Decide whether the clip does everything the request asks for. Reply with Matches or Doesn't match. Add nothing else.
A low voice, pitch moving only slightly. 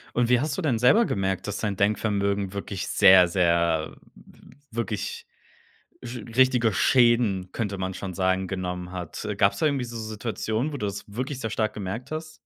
Doesn't match